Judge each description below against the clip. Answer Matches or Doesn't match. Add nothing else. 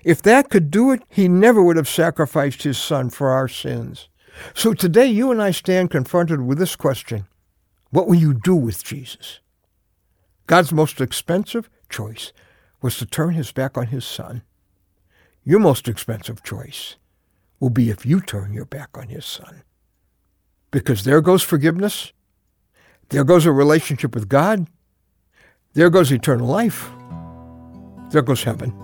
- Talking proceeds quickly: Doesn't match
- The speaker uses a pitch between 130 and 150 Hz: Matches